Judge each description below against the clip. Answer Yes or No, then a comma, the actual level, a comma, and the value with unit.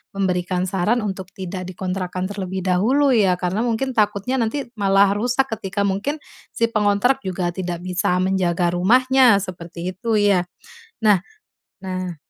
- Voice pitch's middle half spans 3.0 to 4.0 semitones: Yes, average, 3.4 semitones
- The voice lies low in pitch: No, high, 195 Hz